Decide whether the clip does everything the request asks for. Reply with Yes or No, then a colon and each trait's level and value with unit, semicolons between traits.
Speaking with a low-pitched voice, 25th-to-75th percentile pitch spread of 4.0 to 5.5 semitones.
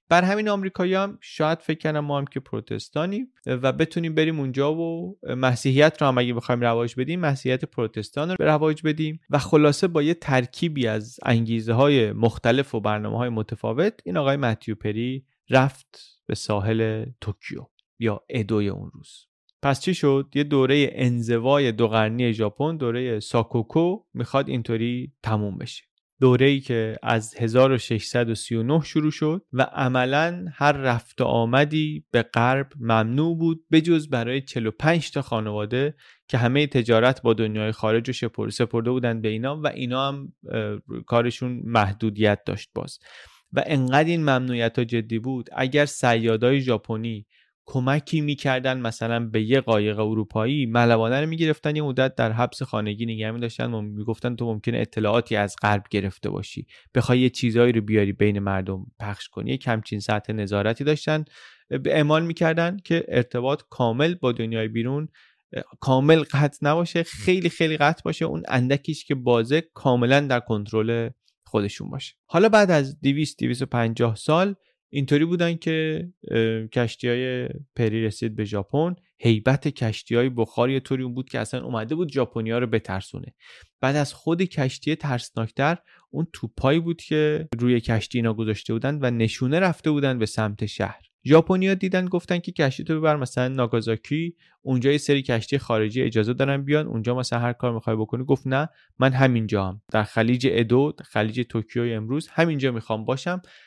Yes: low, 130 Hz; average, 4.6 semitones